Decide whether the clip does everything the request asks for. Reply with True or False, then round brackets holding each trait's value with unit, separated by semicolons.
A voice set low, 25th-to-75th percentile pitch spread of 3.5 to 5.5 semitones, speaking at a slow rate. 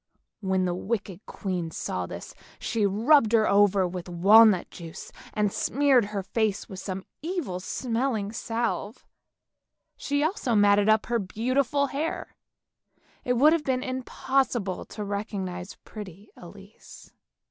False (210 Hz; 4.6 semitones; 130 wpm)